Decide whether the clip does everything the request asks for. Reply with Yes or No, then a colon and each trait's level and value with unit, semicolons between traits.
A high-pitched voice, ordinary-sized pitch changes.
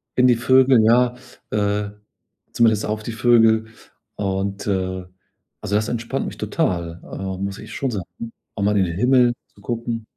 No: low, 110 Hz; average, 3.3 semitones